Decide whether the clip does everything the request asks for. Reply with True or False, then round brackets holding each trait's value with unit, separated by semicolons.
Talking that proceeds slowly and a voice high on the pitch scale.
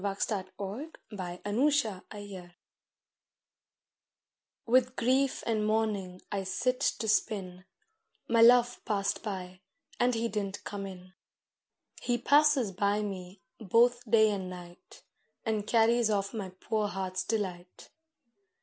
True (115 wpm; 210 Hz)